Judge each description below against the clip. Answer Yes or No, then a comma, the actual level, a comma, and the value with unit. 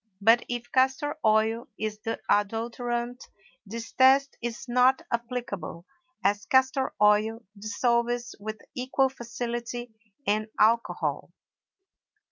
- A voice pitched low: No, high, 235 Hz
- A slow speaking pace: Yes, slow, 100 wpm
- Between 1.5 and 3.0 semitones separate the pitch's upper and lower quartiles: Yes, narrow, 2.5 semitones